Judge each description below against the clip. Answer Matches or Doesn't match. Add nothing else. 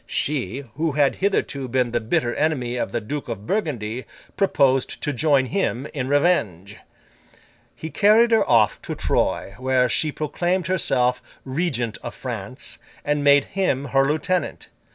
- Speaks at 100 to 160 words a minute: Matches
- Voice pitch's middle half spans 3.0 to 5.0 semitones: Matches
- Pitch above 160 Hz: Doesn't match